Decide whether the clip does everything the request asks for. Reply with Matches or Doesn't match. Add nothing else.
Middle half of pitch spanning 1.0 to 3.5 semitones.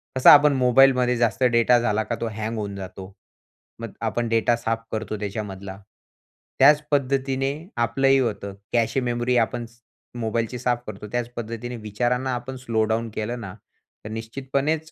Matches